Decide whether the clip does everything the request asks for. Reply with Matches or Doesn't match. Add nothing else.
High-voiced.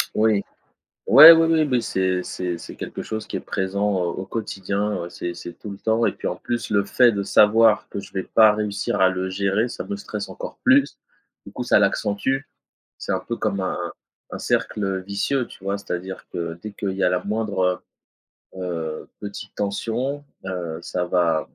Doesn't match